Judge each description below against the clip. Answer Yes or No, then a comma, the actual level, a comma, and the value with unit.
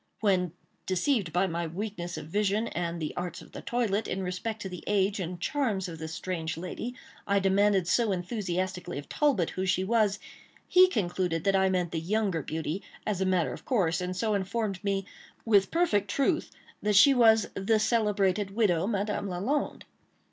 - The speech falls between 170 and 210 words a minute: Yes, average, 180 wpm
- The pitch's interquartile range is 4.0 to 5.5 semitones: No, average, 3.2 semitones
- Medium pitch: No, high, 195 Hz